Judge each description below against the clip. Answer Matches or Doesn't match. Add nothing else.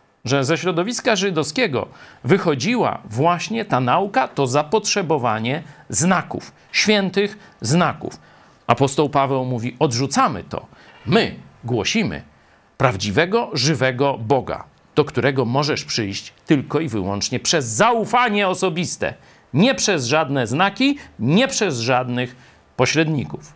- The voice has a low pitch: Doesn't match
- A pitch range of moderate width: Doesn't match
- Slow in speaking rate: Matches